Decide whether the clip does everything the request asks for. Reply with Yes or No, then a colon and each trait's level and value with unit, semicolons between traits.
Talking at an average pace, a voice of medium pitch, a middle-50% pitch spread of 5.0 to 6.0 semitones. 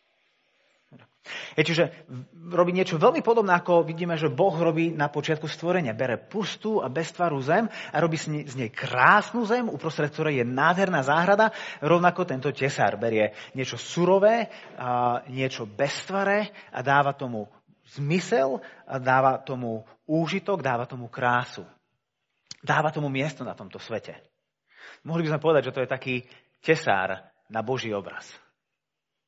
Yes: average, 135 wpm; medium, 155 Hz; average, 5.3 semitones